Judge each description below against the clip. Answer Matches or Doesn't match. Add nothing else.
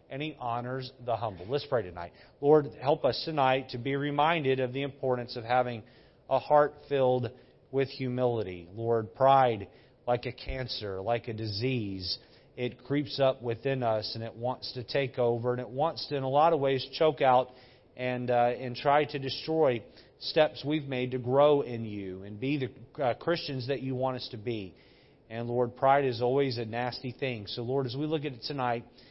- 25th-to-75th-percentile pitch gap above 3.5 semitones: Doesn't match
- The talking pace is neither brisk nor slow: Matches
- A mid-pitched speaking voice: Doesn't match